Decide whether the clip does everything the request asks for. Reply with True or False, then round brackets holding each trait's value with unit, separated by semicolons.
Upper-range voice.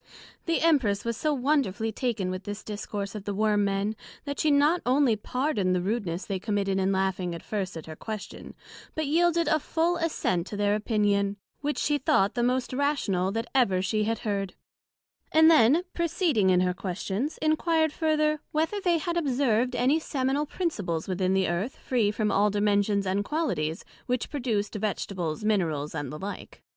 True (215 Hz)